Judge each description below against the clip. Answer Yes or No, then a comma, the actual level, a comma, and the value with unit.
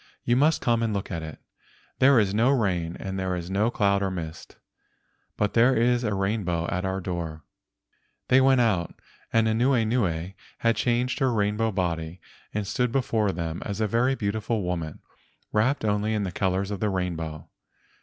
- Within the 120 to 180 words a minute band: Yes, average, 175 wpm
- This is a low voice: Yes, low, 105 Hz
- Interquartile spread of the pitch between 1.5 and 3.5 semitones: No, average, 4.3 semitones